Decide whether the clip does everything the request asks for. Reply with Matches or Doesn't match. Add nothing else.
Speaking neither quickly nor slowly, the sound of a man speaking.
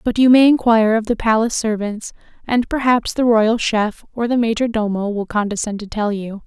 Doesn't match